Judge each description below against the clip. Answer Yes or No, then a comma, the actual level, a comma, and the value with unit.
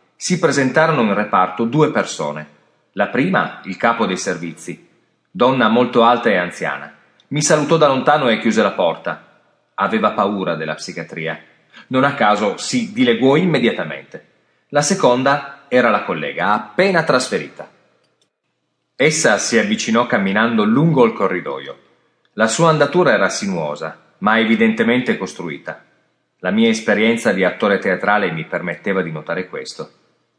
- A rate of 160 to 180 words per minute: No, average, 135 wpm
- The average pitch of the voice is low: Yes, low, 120 Hz